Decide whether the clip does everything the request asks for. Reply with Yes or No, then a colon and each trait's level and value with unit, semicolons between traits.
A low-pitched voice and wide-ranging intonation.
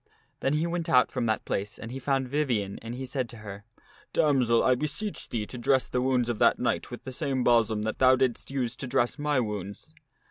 No: low, 125 Hz; average, 2.8 semitones